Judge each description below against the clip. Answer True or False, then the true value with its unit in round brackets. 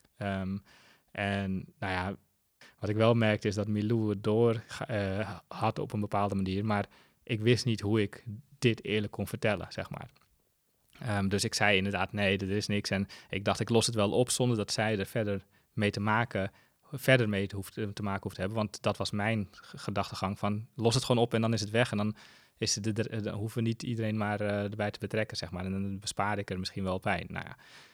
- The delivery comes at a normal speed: False (225 wpm)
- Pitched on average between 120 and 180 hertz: False (105 Hz)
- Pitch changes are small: True (2.1 semitones)